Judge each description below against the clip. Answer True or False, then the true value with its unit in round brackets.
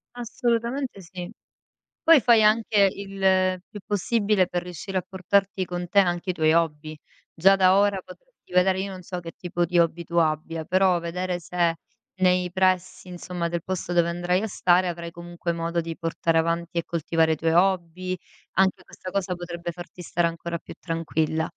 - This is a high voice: False (180 Hz)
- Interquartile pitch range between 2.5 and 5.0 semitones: False (2.1 semitones)